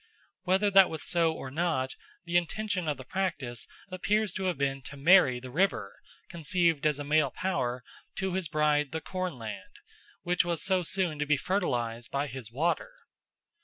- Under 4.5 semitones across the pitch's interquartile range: No, average, 5.1 semitones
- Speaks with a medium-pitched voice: Yes, medium, 160 Hz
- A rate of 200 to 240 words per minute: No, average, 170 wpm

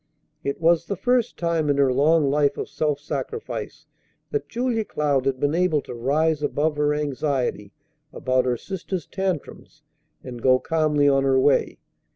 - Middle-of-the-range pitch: Yes, medium, 150 Hz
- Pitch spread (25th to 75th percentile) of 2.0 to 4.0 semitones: Yes, average, 3.6 semitones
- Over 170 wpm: No, average, 165 wpm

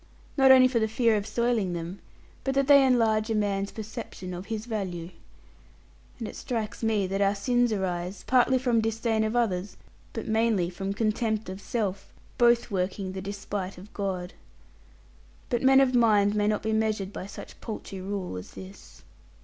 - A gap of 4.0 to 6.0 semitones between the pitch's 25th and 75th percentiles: No, average, 3.2 semitones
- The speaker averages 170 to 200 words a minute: Yes, average, 175 wpm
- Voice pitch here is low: No, high, 215 Hz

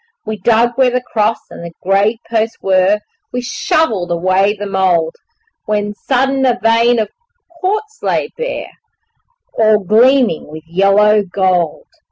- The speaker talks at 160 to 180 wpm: No, average, 140 wpm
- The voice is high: Yes, high, 215 Hz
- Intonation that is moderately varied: Yes, average, 4.2 semitones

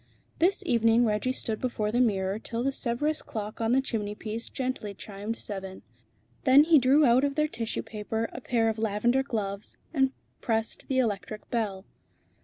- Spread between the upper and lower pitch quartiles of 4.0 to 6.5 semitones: No, average, 3.5 semitones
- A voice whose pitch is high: Yes, high, 230 Hz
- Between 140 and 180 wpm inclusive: Yes, average, 170 wpm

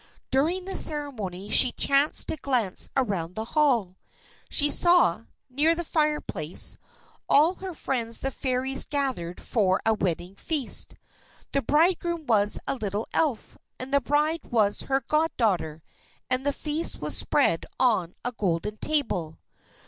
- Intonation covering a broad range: Yes, wide, 6.6 semitones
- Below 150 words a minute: Yes, average, 140 wpm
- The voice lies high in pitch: Yes, very high, 255 Hz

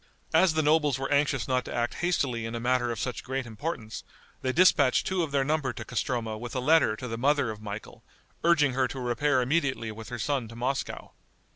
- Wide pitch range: No, average, 3.7 semitones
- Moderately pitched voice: No, low, 130 Hz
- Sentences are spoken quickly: Yes, fast, 220 wpm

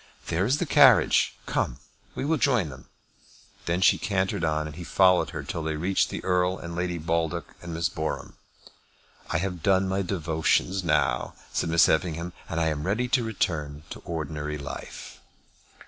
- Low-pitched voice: Yes, very low, 85 Hz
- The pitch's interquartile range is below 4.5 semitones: Yes, average, 3.4 semitones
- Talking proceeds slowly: No, average, 170 wpm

